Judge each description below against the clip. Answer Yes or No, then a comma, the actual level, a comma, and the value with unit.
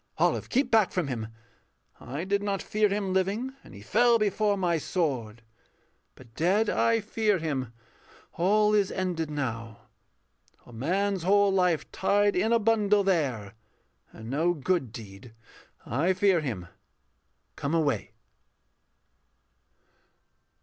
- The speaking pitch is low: No, medium, 185 Hz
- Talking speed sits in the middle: No, slow, 130 wpm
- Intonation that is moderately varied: No, wide, 6.9 semitones